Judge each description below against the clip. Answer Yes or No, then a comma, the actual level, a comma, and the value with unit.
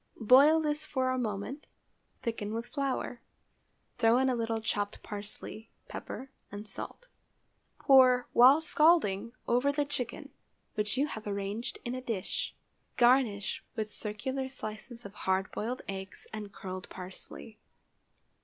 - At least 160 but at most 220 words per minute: No, slow, 135 wpm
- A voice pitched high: Yes, high, 230 Hz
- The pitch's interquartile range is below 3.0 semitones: No, average, 4.1 semitones